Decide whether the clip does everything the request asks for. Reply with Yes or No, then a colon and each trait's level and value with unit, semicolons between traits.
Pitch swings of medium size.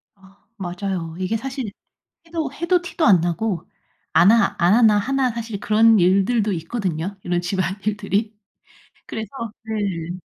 Yes: average, 3.7 semitones